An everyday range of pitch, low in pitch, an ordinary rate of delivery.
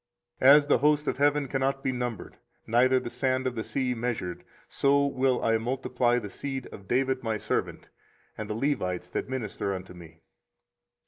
Yes: average, 3.3 semitones; low, 125 Hz; average, 180 wpm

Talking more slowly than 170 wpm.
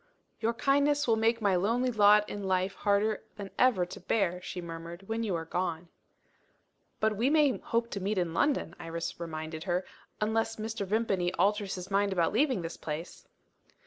No: average, 175 wpm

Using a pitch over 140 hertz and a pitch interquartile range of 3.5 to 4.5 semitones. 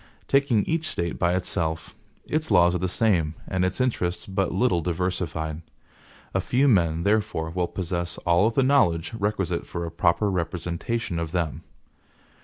No: very low, 90 Hz; average, 3.9 semitones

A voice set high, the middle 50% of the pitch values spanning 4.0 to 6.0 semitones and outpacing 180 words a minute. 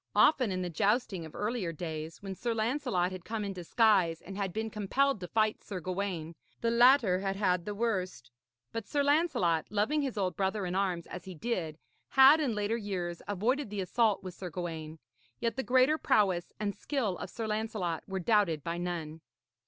Yes: high, 200 Hz; average, 4.3 semitones; average, 190 wpm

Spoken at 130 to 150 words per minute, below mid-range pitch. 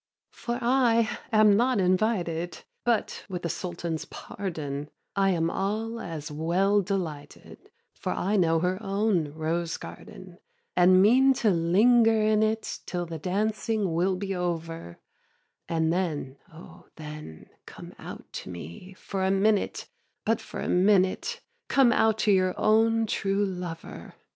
No: average, 145 wpm; high, 190 Hz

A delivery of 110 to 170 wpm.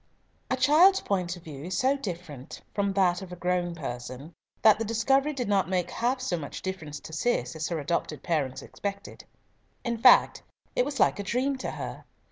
No: average, 195 wpm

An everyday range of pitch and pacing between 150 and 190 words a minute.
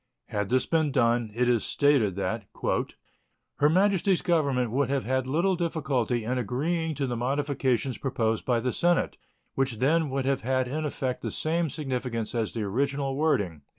Yes: average, 3.8 semitones; average, 170 wpm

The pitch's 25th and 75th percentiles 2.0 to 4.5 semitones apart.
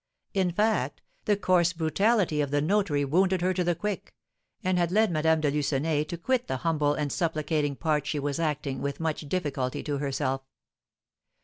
Yes: average, 3.8 semitones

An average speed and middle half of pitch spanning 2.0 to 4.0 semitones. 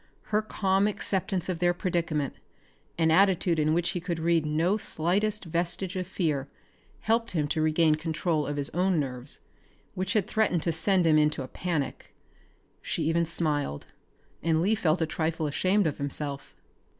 Yes: average, 165 wpm; average, 3.3 semitones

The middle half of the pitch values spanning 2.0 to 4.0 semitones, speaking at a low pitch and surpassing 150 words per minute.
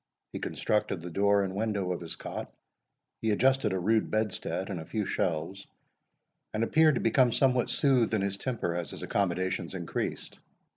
Yes: average, 3.5 semitones; low, 100 Hz; average, 175 wpm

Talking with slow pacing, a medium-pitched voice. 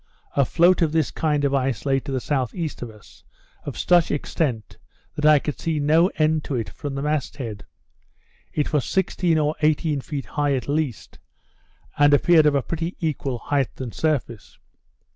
No: average, 180 wpm; medium, 145 Hz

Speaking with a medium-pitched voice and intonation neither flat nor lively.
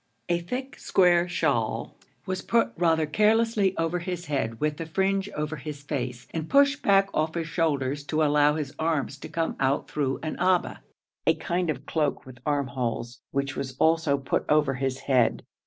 Yes: medium, 155 Hz; average, 4.1 semitones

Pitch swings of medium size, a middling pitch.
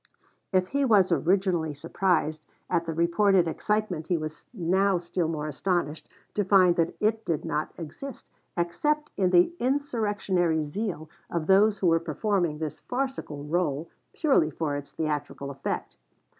Yes: average, 4.3 semitones; medium, 175 Hz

